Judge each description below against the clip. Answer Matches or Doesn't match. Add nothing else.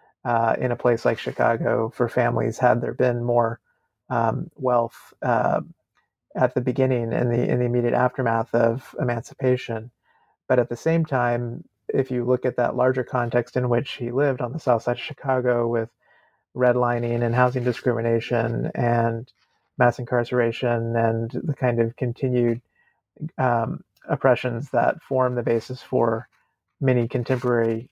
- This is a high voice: Doesn't match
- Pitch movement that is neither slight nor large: Doesn't match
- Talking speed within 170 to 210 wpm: Doesn't match